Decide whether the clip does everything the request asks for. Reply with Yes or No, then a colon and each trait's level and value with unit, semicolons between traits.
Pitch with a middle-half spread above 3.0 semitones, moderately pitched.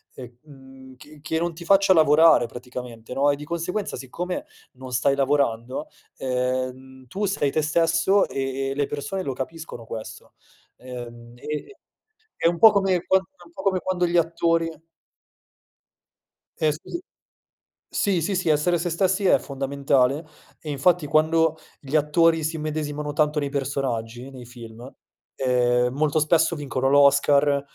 Yes: average, 4.2 semitones; medium, 145 Hz